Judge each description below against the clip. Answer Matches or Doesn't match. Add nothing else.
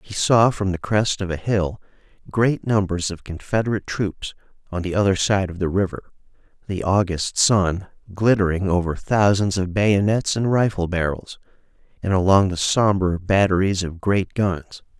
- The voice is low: Matches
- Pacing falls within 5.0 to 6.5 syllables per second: Doesn't match